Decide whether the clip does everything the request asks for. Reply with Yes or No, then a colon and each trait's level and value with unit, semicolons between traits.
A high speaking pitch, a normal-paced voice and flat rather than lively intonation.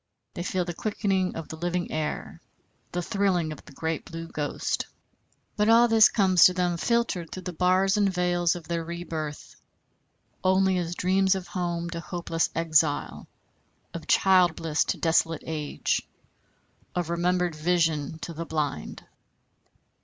No: medium, 175 Hz; average, 150 wpm; narrow, 2.3 semitones